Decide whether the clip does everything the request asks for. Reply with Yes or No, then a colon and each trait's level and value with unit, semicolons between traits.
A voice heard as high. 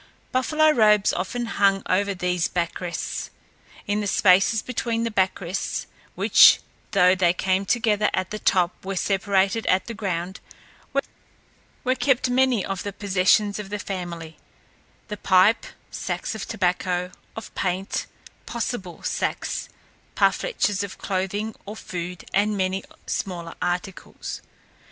Yes: high, 195 Hz